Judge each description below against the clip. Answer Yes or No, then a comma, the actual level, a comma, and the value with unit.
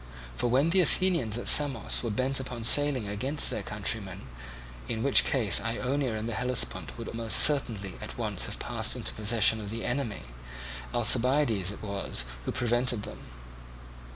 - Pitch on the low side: Yes, low, 120 Hz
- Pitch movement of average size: Yes, average, 3.7 semitones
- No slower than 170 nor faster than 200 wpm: No, average, 160 wpm